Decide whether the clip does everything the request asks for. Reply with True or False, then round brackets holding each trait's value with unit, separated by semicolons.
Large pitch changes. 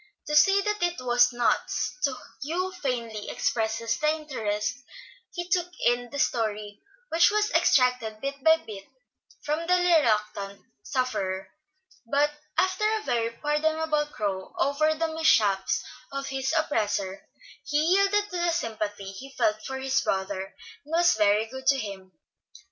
True (6.9 semitones)